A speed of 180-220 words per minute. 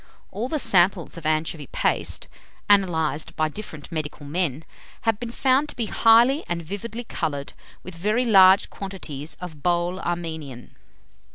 No: average, 145 wpm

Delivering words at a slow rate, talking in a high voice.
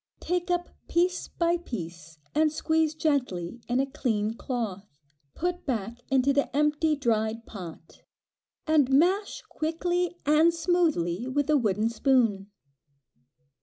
Yes: slow, 125 wpm; very high, 275 Hz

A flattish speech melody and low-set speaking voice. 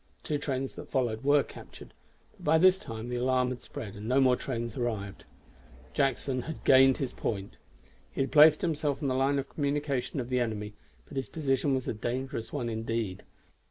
No: average, 3.2 semitones; low, 130 Hz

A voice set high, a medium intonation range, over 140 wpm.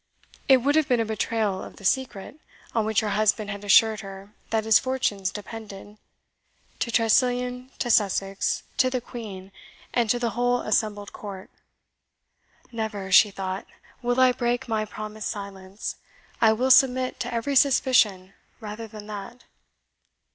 Yes: high, 220 Hz; average, 3.3 semitones; average, 150 wpm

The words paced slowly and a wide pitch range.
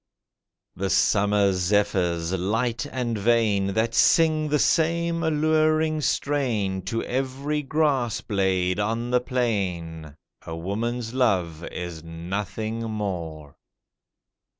Yes: slow, 105 wpm; wide, 6.0 semitones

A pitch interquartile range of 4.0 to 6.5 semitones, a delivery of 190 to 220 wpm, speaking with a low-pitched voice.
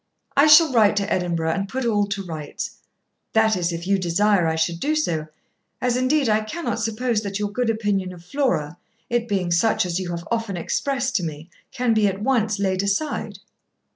No: average, 5.0 semitones; average, 200 wpm; high, 205 Hz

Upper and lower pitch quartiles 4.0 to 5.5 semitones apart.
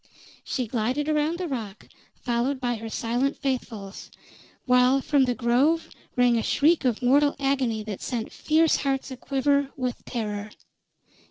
No: average, 3.1 semitones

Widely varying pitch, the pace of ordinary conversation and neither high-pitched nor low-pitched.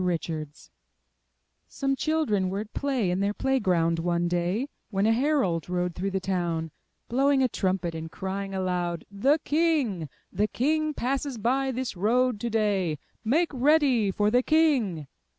No: wide, 6.9 semitones; average, 155 wpm; high, 210 Hz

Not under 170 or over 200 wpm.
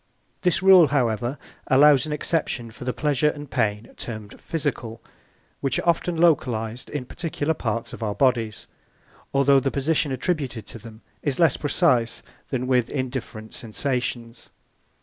No: average, 150 wpm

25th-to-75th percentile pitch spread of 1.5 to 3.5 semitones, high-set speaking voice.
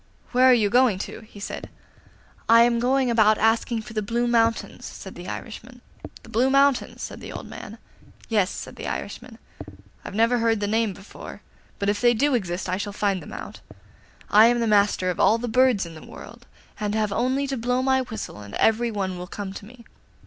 Yes: average, 2.9 semitones; high, 225 Hz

